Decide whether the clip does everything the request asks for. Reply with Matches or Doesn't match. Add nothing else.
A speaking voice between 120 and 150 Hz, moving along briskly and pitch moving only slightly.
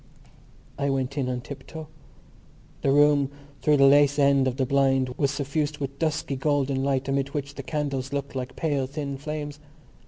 Doesn't match